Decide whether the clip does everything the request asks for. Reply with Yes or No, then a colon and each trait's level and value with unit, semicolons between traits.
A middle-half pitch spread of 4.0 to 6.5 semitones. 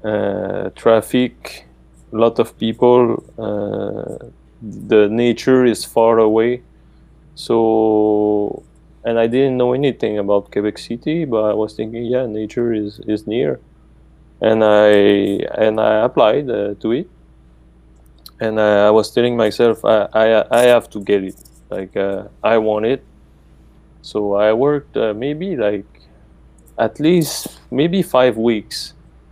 No: average, 2.7 semitones